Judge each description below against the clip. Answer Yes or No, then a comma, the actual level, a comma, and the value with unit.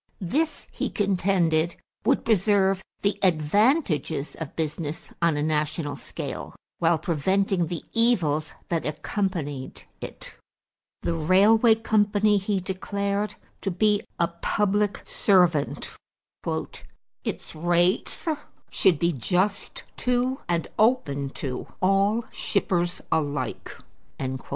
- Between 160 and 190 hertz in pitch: Yes, medium, 185 Hz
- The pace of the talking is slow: Yes, slow, 105 wpm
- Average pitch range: Yes, average, 4.4 semitones